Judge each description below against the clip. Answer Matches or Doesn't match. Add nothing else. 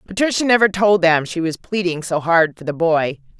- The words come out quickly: Matches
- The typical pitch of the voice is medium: Matches